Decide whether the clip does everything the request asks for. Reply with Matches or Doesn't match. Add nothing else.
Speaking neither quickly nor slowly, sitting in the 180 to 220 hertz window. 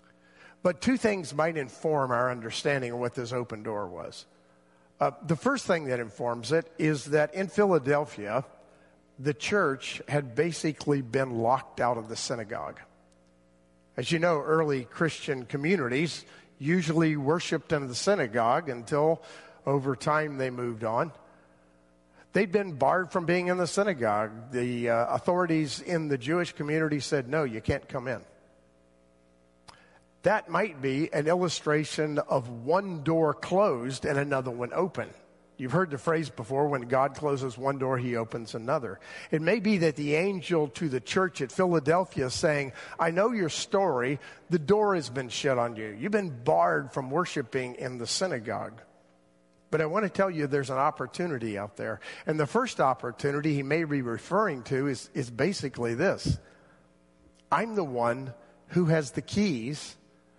Doesn't match